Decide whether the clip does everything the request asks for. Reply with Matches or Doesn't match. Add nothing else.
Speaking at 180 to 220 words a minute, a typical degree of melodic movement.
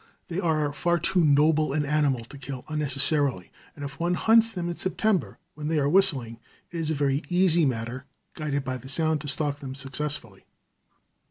Matches